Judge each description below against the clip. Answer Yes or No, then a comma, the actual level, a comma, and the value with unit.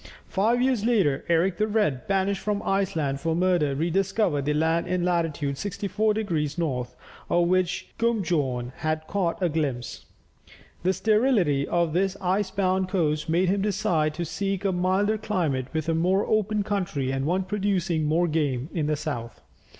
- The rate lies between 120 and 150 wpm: No, average, 165 wpm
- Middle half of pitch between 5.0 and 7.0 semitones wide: No, average, 4.4 semitones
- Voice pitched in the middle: Yes, medium, 175 Hz